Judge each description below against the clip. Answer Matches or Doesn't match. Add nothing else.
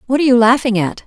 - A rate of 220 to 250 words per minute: Doesn't match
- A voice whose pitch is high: Matches